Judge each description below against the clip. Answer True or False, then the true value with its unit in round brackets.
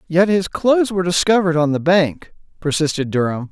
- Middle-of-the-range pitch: True (165 Hz)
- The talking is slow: False (170 wpm)